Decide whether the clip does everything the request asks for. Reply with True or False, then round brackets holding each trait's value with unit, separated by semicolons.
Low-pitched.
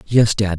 True (105 Hz)